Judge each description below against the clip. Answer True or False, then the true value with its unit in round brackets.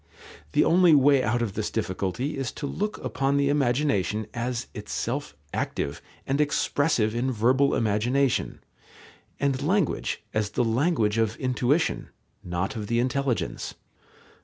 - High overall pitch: False (125 Hz)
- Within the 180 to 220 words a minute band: False (135 wpm)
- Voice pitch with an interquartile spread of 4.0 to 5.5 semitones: True (4.3 semitones)